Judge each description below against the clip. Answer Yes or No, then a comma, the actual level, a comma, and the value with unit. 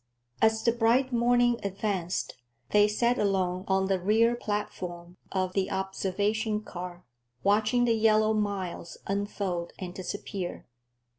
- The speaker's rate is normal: No, slow, 125 wpm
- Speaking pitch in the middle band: No, high, 205 Hz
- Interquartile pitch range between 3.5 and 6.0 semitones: No, average, 3.0 semitones